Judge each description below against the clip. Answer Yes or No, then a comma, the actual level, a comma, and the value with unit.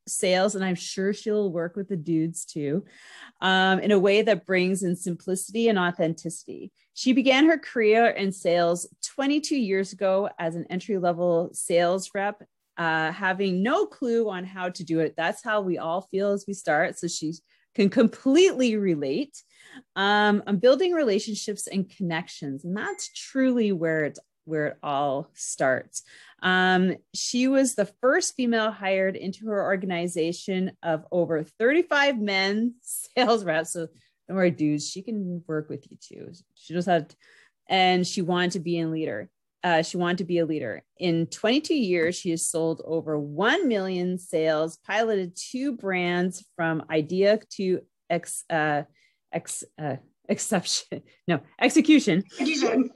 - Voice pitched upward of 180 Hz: Yes, high, 190 Hz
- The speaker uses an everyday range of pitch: Yes, average, 4.0 semitones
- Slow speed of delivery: No, average, 155 wpm